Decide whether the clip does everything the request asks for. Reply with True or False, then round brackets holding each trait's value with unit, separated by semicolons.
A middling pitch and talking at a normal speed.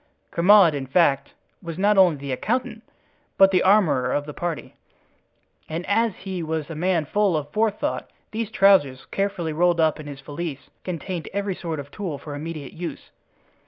True (170 Hz; 170 wpm)